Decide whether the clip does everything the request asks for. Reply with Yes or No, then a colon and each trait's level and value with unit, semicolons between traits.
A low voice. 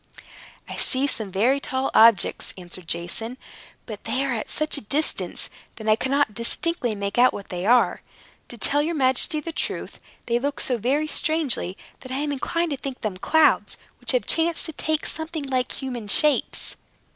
No: very high, 260 Hz